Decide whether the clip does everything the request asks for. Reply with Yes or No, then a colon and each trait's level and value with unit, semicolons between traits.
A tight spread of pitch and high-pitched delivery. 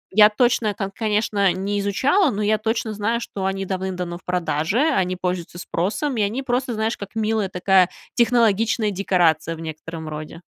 No: average, 3.5 semitones; high, 200 Hz